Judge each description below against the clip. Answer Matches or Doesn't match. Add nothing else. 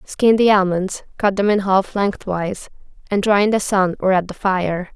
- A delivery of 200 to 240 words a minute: Matches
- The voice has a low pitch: Doesn't match